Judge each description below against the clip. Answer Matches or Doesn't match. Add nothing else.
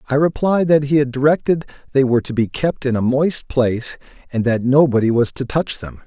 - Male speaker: Matches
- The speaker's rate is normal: Doesn't match